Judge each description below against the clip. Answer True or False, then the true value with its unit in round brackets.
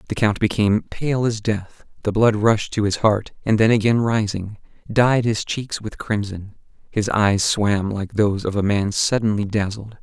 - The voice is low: True (105 Hz)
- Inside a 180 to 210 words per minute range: True (185 wpm)